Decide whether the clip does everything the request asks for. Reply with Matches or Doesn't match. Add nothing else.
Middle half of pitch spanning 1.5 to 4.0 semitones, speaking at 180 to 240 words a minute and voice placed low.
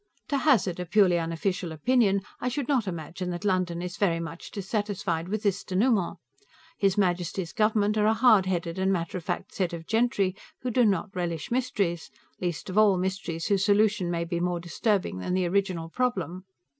Doesn't match